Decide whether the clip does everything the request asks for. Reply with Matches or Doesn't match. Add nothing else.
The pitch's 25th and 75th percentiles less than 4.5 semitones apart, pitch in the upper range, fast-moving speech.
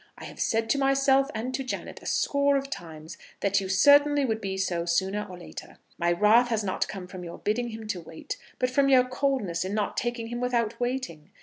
Doesn't match